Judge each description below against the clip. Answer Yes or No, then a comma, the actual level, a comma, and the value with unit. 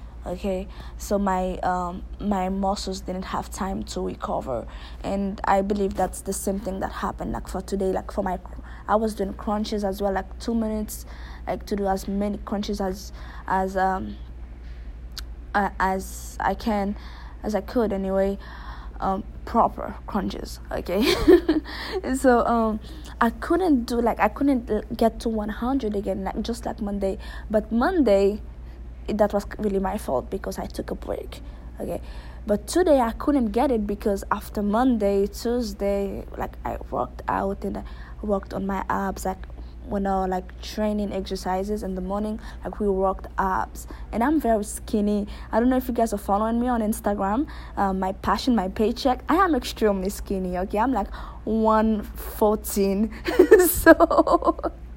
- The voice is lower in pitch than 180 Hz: No, high, 205 Hz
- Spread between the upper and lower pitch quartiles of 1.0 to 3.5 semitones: Yes, average, 3.0 semitones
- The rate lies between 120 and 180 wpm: Yes, average, 165 wpm